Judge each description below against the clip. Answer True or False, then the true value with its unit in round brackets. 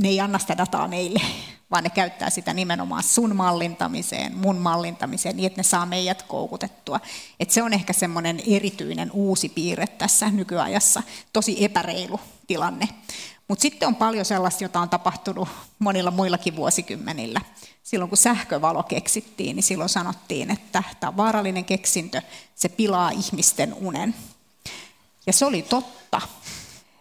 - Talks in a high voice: True (195 Hz)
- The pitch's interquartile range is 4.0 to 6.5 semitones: False (2.9 semitones)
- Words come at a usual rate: True (140 wpm)